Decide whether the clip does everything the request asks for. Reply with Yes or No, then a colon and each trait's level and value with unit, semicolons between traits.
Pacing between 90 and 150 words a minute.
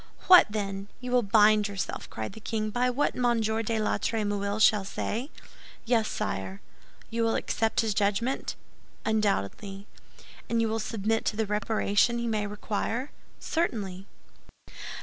Yes: average, 145 wpm